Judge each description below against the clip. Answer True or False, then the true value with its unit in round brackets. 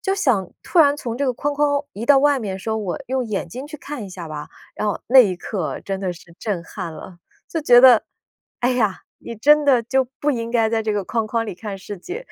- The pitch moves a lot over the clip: True (5.8 semitones)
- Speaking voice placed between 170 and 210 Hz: False (230 Hz)